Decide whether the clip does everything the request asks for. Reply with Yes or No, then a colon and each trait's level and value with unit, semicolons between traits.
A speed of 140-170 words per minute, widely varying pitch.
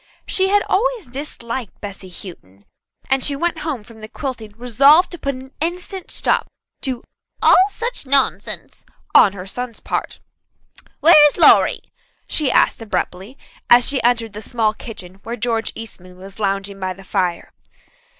Yes: average, 155 wpm; wide, 6.1 semitones